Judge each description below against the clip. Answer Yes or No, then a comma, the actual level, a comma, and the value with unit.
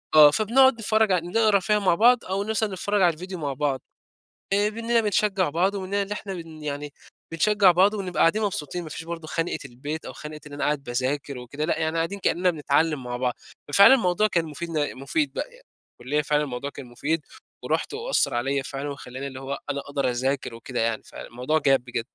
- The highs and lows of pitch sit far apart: Yes, wide, 6.2 semitones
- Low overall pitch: No, medium, 160 Hz